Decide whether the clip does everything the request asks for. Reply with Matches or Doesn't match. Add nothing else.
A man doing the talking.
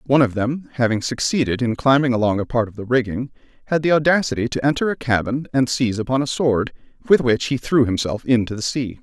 Matches